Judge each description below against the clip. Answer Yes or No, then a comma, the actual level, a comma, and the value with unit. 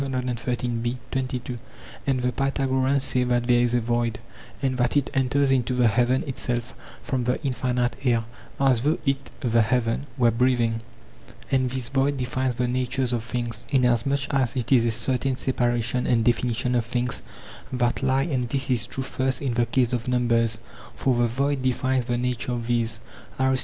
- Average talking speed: Yes, average, 175 wpm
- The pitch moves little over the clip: Yes, narrow, 1.6 semitones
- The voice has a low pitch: Yes, low, 125 Hz